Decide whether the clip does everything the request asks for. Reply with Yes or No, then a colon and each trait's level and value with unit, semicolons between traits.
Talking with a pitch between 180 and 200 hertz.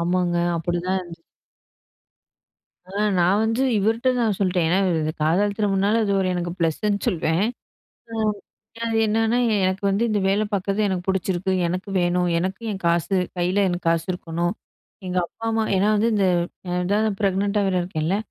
Yes: high, 190 Hz